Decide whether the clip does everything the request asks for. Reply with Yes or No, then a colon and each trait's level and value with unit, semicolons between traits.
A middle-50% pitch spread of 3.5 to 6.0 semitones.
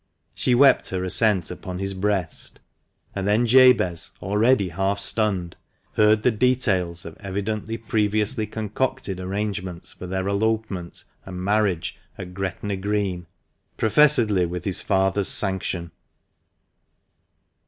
No: average, 2.8 semitones